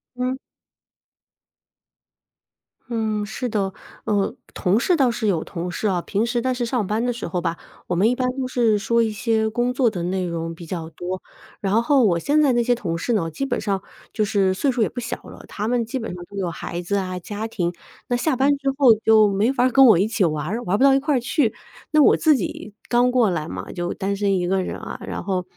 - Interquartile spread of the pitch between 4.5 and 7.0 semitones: Yes, average, 4.9 semitones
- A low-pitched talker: No, high, 215 Hz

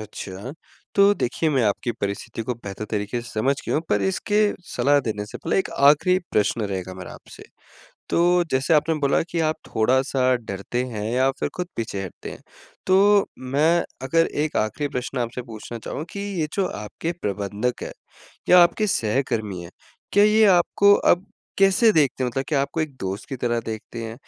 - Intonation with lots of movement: Yes, wide, 7.3 semitones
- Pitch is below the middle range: Yes, low, 130 Hz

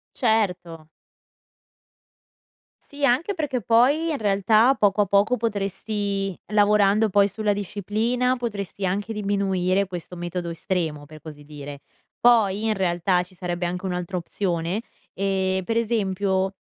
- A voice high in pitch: Yes, high, 200 Hz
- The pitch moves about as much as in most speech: Yes, average, 3.4 semitones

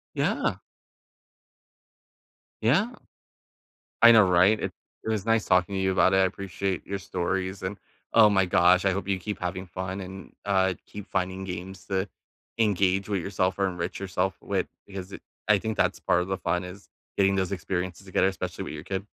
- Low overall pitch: Yes, very low, 95 Hz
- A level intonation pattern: Yes, narrow, 1.3 semitones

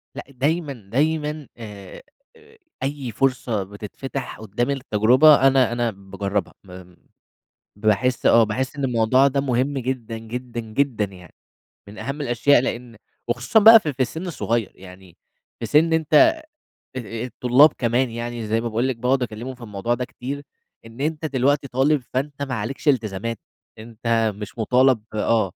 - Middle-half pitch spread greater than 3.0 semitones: Yes, average, 3.8 semitones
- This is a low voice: Yes, low, 125 Hz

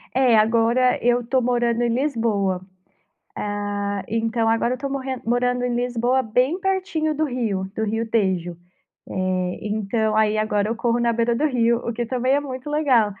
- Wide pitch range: No, average, 2.8 semitones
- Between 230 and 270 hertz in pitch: Yes, high, 235 Hz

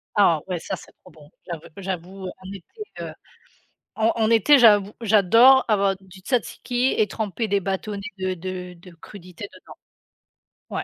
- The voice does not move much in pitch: No, average, 3.1 semitones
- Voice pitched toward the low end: No, high, 195 Hz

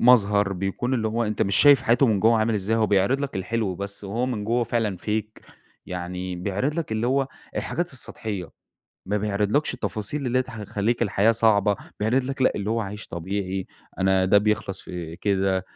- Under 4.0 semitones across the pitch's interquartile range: Yes, average, 3.3 semitones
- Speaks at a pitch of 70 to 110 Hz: Yes, low, 105 Hz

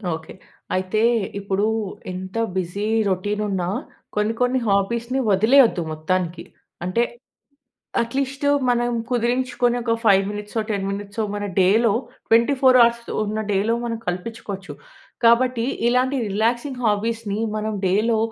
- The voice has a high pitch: Yes, high, 220 Hz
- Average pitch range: Yes, average, 3.4 semitones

